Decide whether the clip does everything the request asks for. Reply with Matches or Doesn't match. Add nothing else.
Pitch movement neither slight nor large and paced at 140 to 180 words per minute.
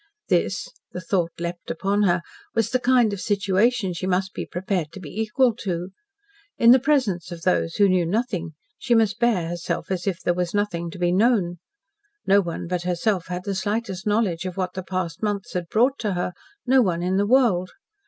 Doesn't match